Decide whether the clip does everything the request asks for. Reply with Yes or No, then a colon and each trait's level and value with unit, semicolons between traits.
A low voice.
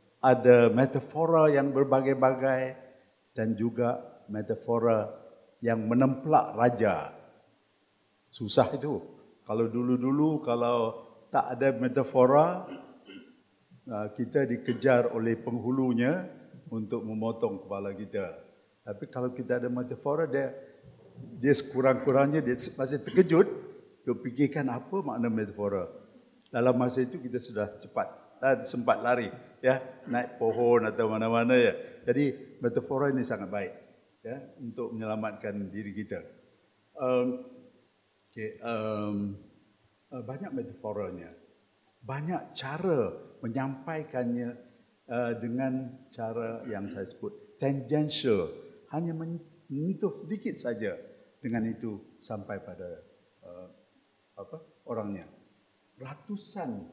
Yes: low, 125 Hz